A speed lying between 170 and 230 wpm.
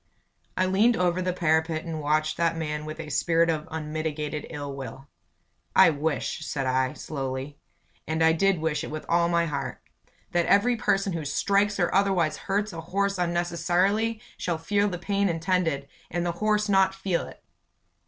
Yes: average, 175 wpm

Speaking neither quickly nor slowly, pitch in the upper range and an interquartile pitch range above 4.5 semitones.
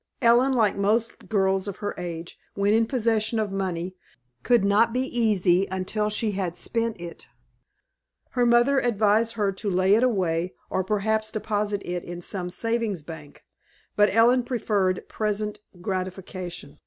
No: average, 150 wpm; high, 205 Hz; average, 3.5 semitones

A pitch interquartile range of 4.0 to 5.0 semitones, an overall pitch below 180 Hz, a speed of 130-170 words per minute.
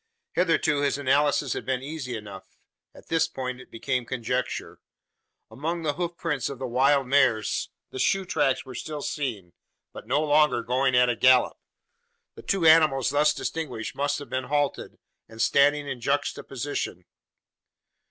No: average, 2.9 semitones; low, 135 Hz; average, 155 wpm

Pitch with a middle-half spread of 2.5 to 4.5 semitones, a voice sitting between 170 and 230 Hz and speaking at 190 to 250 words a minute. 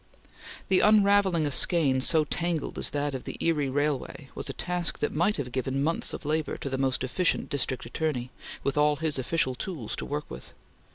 No: average, 3.8 semitones; medium, 150 Hz; average, 195 wpm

